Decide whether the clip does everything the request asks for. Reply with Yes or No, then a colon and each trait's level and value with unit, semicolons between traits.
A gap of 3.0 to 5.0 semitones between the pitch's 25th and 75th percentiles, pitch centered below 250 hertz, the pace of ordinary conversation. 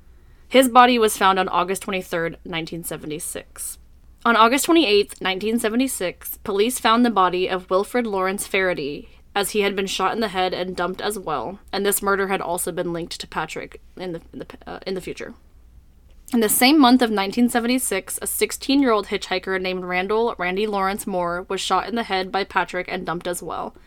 Yes: average, 3.7 semitones; high, 190 Hz; average, 190 wpm